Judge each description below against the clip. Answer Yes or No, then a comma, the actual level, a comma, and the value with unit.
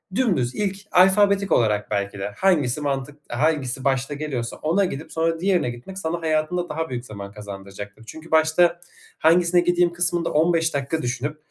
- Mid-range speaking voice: Yes, medium, 155 Hz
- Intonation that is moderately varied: No, wide, 5.9 semitones